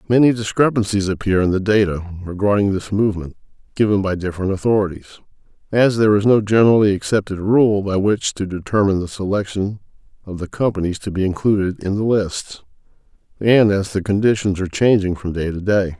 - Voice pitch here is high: No, low, 100 Hz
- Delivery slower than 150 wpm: No, average, 170 wpm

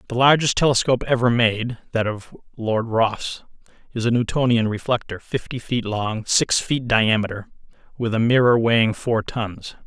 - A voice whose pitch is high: No, low, 115 Hz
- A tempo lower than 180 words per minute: Yes, average, 150 wpm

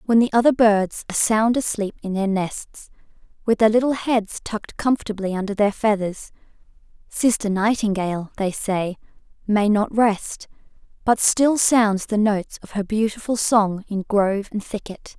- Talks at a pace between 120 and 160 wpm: Yes, average, 155 wpm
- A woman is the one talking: Yes, female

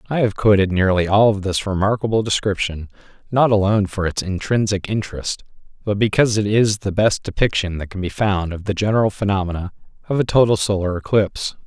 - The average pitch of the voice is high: No, low, 100 Hz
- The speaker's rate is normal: Yes, average, 180 wpm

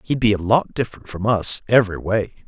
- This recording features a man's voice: Yes, male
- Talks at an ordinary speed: No, fast, 220 wpm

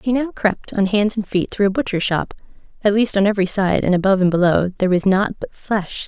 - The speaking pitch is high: Yes, high, 200 Hz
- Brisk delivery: Yes, fast, 245 wpm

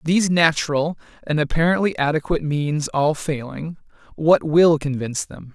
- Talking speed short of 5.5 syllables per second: Yes, 5.0 syllables/s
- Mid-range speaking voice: Yes, medium, 155 Hz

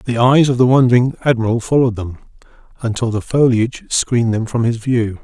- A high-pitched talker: No, low, 120 Hz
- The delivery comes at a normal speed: Yes, average, 185 wpm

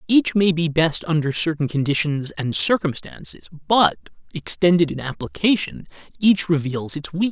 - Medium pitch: Yes, medium, 160 Hz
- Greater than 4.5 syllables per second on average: Yes, 5.1 syllables/s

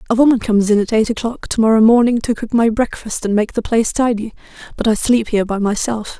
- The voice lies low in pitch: No, high, 225 Hz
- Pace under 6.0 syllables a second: No, 6.3 syllables/s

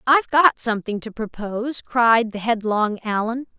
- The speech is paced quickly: No, average, 150 wpm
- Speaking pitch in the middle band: No, high, 230 Hz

